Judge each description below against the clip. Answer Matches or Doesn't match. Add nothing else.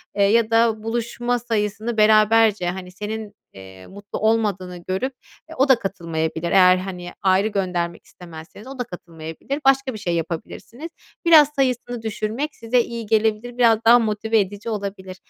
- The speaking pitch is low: Doesn't match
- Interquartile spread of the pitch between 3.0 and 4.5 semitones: Matches